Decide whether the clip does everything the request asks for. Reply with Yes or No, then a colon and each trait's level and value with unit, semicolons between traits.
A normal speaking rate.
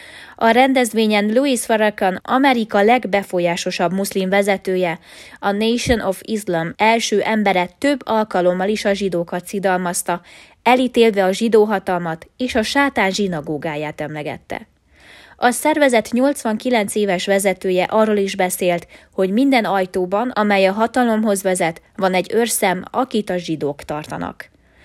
Yes: average, 120 wpm